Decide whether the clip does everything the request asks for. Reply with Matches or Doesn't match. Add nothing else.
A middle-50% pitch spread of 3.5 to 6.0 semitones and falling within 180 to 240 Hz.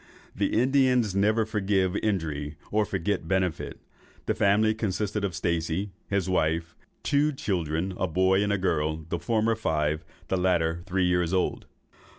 Doesn't match